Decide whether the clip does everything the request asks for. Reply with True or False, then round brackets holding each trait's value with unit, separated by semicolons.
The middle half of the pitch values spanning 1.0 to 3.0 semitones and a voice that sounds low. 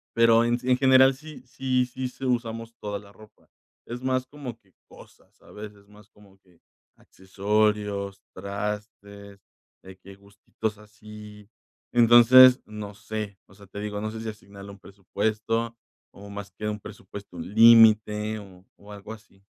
True (2.4 semitones; 105 Hz)